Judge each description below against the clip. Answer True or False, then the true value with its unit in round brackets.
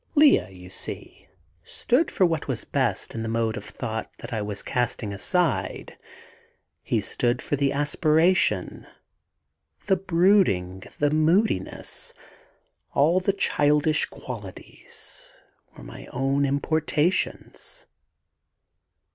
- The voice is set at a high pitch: False (145 Hz)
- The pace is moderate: False (110 wpm)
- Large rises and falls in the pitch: True (7.7 semitones)